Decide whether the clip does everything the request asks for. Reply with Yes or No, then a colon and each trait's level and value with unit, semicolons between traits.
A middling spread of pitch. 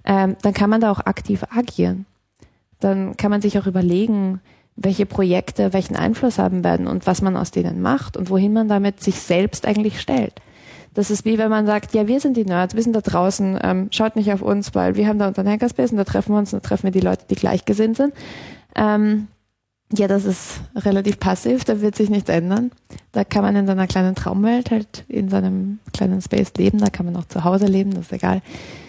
No: narrow, 2.3 semitones